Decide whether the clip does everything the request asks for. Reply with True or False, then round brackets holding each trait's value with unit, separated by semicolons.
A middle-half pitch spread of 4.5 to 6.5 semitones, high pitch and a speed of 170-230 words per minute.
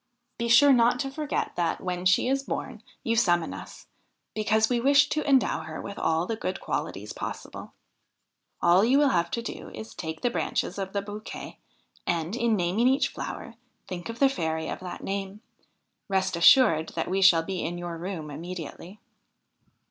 True (5.3 semitones; 195 Hz; 185 wpm)